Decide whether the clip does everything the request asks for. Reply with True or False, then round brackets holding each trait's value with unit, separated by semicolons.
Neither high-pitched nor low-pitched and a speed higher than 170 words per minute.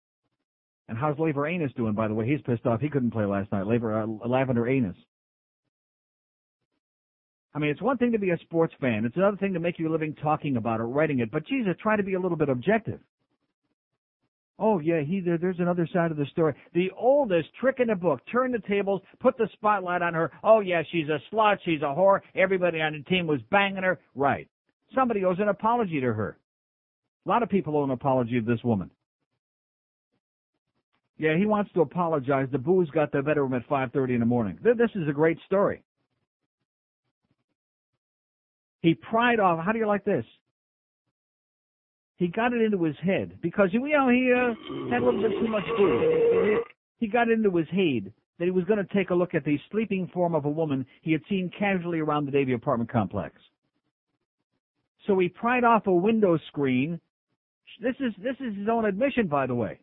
True (170 Hz; 200 wpm)